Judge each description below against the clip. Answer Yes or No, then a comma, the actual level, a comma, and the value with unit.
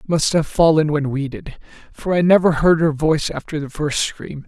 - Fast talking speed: Yes, fast, 215 wpm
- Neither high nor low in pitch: Yes, medium, 155 Hz